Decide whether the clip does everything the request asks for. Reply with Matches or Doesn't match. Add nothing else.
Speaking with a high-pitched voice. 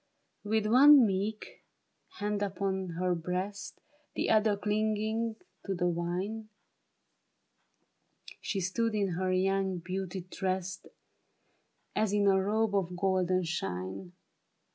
Matches